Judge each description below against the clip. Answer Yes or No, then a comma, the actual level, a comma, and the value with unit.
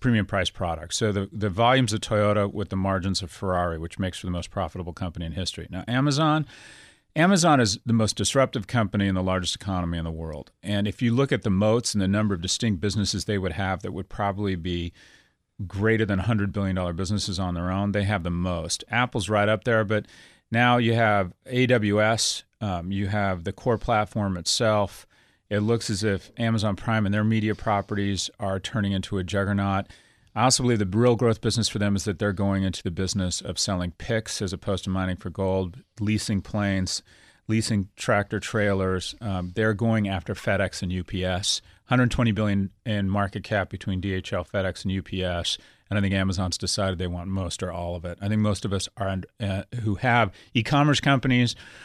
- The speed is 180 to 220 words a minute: Yes, average, 200 wpm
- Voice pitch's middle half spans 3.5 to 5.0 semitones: No, average, 2.8 semitones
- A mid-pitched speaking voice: No, low, 100 Hz